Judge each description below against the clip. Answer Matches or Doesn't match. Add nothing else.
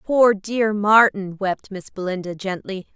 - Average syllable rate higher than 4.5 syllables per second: Doesn't match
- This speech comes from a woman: Matches